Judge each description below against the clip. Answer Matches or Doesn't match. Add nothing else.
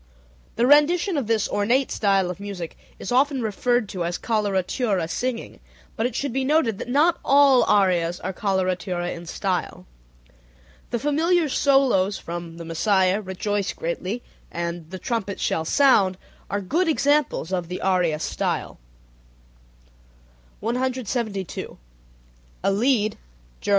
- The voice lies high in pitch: Matches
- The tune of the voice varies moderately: Doesn't match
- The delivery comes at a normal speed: Doesn't match